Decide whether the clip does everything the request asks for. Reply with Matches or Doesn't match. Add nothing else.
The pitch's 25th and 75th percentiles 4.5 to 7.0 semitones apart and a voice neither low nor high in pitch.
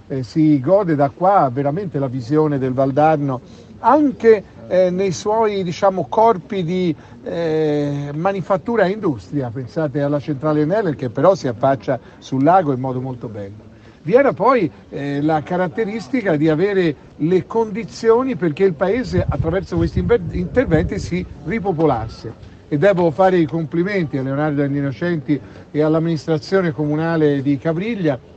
Matches